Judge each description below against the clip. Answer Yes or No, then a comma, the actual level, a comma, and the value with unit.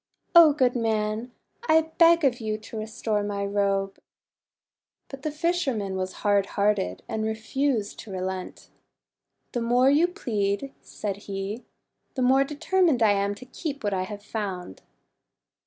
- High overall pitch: Yes, high, 220 Hz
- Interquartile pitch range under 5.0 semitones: No, average, 5.3 semitones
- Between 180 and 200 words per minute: No, average, 150 wpm